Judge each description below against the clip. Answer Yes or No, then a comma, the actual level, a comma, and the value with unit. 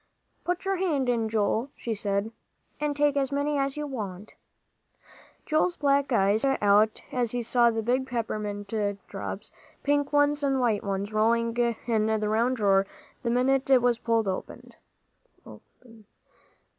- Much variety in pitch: No, average, 4.4 semitones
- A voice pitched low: No, high, 235 Hz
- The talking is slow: No, average, 145 wpm